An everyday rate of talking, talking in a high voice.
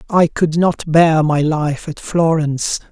No: average, 165 wpm; medium, 160 Hz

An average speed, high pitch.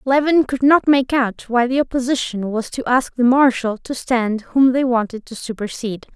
Yes: average, 195 wpm; very high, 250 Hz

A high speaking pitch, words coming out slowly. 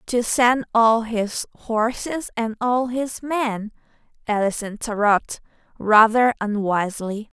Yes: high, 225 Hz; slow, 105 wpm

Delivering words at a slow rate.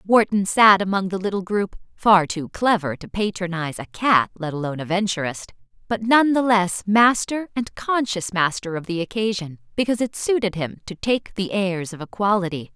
No: average, 180 wpm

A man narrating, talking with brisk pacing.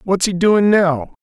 No: male; average, 195 wpm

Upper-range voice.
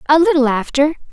Yes: very high, 290 Hz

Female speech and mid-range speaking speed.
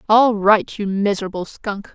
Yes: female; average, 155 wpm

